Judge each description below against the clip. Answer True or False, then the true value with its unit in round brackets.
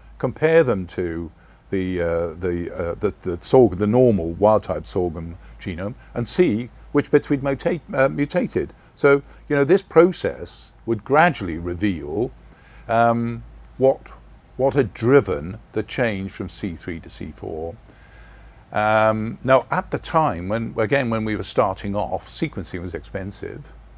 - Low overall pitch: True (110 Hz)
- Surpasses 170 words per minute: False (145 wpm)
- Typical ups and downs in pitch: False (6.6 semitones)